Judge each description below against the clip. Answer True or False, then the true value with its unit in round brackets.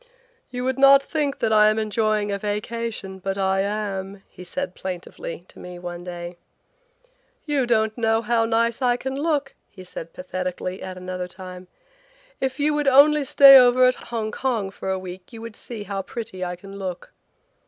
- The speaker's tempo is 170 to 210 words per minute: True (185 wpm)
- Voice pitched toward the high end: True (215 Hz)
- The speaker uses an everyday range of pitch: True (5.0 semitones)